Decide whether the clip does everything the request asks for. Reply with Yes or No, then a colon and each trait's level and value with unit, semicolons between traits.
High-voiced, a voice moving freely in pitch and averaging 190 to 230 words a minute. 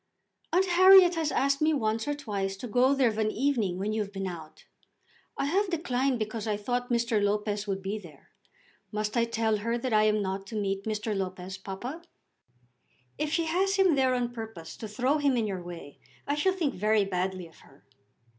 Yes: high, 220 Hz; wide, 5.7 semitones; fast, 205 wpm